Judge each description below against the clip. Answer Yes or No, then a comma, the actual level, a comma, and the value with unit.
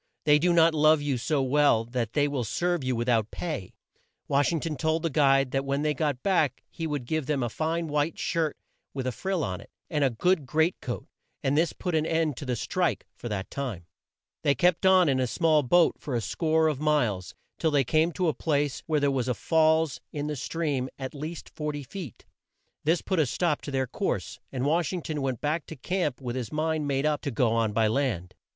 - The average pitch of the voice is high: No, medium, 145 Hz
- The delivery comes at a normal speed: No, fast, 230 wpm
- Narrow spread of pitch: No, average, 3.7 semitones